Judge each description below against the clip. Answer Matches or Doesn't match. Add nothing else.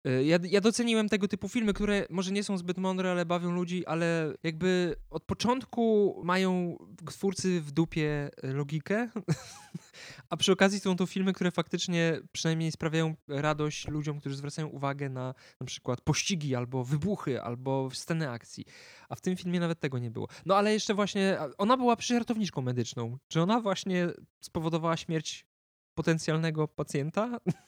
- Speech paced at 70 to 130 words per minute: Doesn't match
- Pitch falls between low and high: Matches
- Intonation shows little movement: Doesn't match